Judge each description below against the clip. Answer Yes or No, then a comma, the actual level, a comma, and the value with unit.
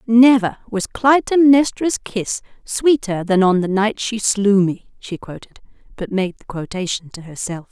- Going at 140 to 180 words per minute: Yes, average, 155 wpm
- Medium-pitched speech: No, high, 210 Hz